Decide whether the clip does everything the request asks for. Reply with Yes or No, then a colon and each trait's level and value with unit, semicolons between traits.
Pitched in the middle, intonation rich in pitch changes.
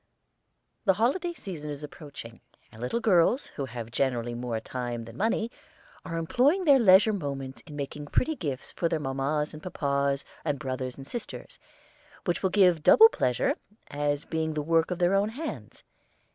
Yes: medium, 150 Hz; wide, 6.2 semitones